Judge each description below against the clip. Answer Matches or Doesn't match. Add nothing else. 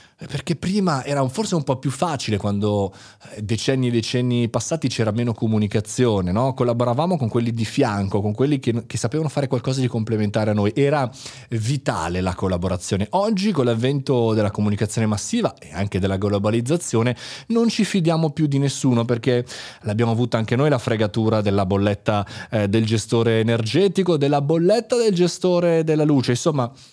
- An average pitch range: Matches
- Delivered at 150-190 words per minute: Matches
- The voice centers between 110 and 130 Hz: Matches